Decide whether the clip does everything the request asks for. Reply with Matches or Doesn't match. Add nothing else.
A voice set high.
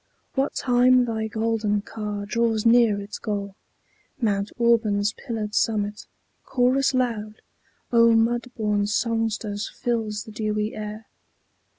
Matches